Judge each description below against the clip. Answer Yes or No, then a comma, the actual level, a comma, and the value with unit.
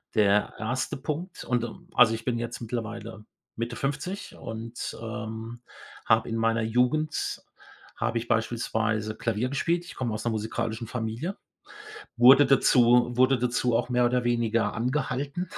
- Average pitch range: No, narrow, 2.1 semitones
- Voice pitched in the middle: No, low, 120 Hz